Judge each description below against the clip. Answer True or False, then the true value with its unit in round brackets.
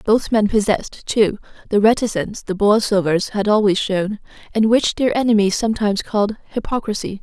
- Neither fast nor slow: True (150 wpm)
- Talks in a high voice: True (210 Hz)